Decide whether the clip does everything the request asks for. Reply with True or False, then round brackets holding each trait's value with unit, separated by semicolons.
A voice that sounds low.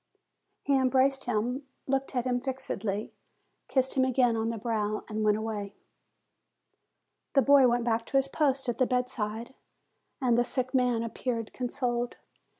False (245 Hz)